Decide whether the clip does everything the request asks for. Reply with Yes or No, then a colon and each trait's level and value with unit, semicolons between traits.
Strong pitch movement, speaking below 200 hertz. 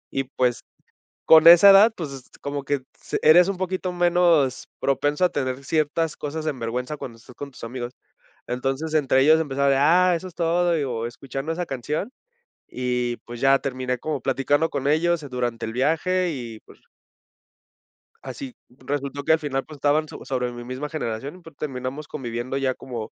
No: average, 4.0 semitones; medium, 140 Hz